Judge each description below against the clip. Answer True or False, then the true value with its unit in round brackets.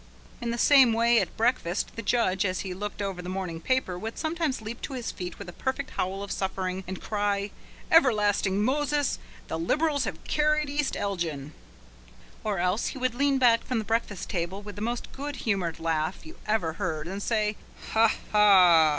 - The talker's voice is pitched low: False (210 Hz)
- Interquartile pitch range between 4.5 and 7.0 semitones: True (5.4 semitones)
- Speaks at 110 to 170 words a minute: False (190 wpm)